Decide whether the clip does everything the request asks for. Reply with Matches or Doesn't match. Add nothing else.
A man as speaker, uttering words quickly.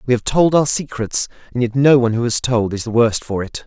Matches